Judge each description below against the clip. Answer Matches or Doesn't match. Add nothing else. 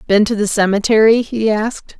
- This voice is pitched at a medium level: Doesn't match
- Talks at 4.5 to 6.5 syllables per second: Matches